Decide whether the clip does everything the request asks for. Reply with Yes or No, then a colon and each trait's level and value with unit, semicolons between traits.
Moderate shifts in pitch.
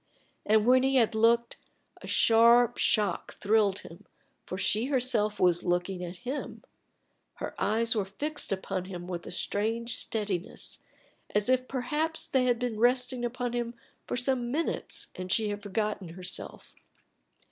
Yes: average, 4.0 semitones